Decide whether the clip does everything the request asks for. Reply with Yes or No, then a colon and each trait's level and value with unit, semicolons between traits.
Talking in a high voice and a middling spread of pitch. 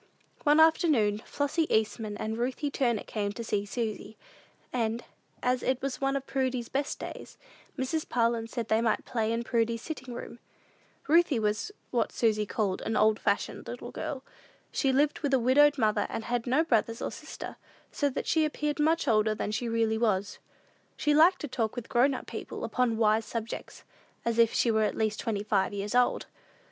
Yes: high, 235 Hz; average, 3.8 semitones